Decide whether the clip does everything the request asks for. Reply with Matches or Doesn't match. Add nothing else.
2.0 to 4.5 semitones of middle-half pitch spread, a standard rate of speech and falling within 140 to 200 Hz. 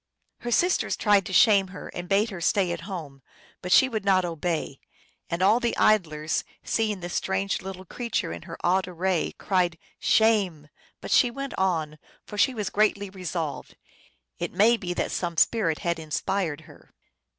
Matches